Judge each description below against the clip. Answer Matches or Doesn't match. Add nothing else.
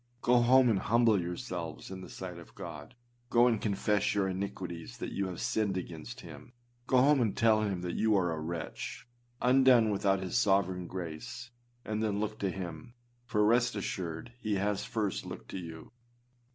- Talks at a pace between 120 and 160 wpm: Doesn't match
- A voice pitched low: Matches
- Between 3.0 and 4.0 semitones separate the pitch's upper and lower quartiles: Doesn't match